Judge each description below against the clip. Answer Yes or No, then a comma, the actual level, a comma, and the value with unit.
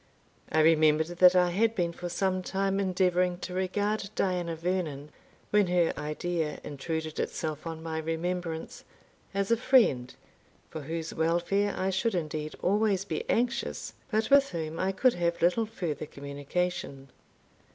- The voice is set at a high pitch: No, medium, 175 Hz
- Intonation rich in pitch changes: No, average, 3.3 semitones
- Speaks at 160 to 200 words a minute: No, average, 145 wpm